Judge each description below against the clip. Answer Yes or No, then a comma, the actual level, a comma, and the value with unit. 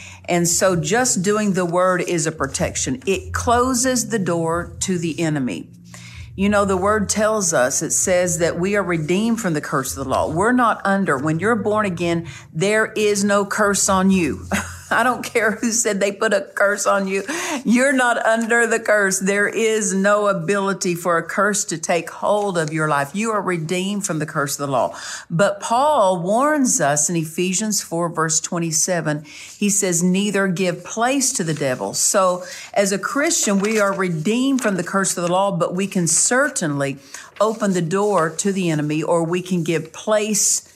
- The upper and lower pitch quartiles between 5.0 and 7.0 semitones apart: No, average, 3.9 semitones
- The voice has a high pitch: Yes, high, 195 Hz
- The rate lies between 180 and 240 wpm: Yes, average, 190 wpm